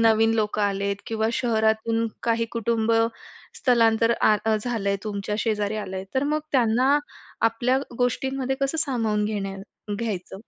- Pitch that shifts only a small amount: Yes, narrow, 2.2 semitones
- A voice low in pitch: No, high, 225 Hz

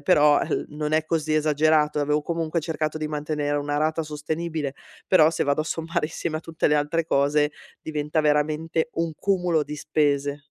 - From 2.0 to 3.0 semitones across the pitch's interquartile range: No, narrow, 1.4 semitones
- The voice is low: No, medium, 155 Hz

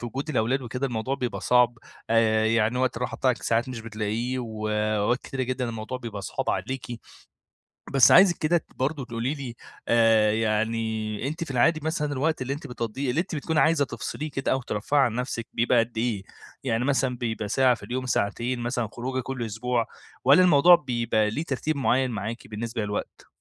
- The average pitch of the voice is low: Yes, low, 120 Hz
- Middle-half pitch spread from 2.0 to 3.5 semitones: Yes, average, 3.0 semitones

